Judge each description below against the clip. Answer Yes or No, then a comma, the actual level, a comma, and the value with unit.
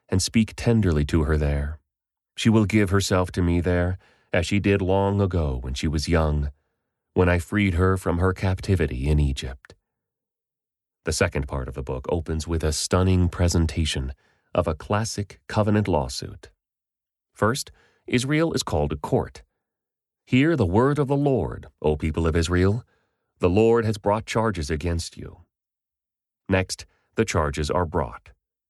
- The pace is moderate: Yes, average, 155 wpm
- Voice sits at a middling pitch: No, very low, 90 Hz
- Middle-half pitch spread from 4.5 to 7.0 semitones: Yes, average, 4.8 semitones